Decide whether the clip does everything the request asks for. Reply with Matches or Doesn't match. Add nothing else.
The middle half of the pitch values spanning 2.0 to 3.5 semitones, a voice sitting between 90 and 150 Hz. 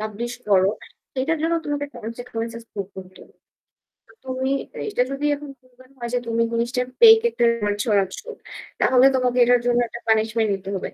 Doesn't match